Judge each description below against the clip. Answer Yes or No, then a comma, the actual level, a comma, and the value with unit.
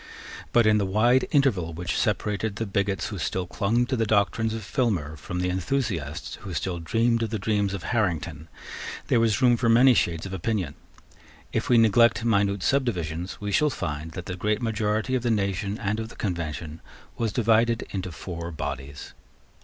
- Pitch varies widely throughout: No, average, 4.3 semitones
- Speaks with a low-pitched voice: Yes, low, 105 Hz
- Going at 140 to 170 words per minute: No, average, 180 wpm